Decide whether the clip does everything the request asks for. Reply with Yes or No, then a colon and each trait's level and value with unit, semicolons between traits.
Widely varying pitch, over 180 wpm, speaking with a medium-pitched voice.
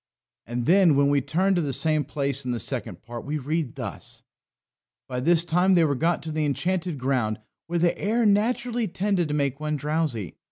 No: average, 4.3 semitones; average, 200 wpm; medium, 155 Hz